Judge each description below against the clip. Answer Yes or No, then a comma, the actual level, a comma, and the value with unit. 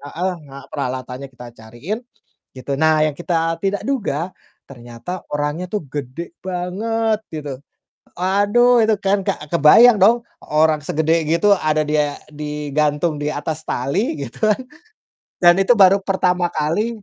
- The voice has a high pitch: No, medium, 160 Hz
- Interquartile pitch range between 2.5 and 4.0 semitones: No, average, 4.9 semitones